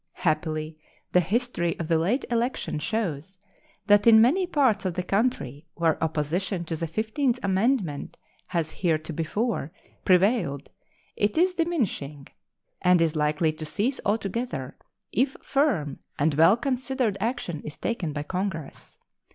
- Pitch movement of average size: No, wide, 6.9 semitones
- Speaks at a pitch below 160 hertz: No, medium, 185 Hz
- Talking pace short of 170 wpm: Yes, slow, 135 wpm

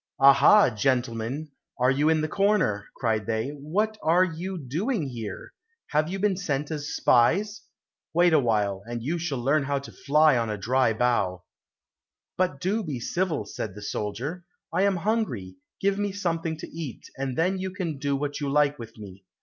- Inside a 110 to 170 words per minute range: No, average, 180 wpm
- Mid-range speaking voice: Yes, medium, 145 Hz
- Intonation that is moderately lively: No, wide, 6.9 semitones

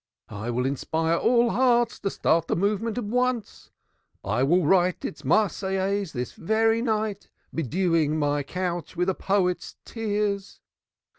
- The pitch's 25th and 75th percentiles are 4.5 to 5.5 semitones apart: Yes, average, 5.1 semitones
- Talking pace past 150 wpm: No, average, 140 wpm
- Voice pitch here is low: No, high, 190 Hz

